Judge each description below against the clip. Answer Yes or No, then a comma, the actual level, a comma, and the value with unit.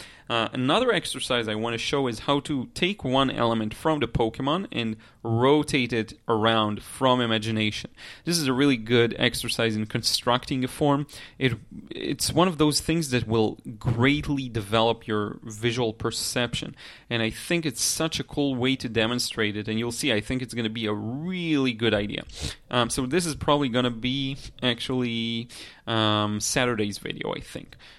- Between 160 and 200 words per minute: Yes, average, 180 wpm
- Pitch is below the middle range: Yes, low, 120 Hz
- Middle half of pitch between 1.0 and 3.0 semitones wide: No, average, 3.4 semitones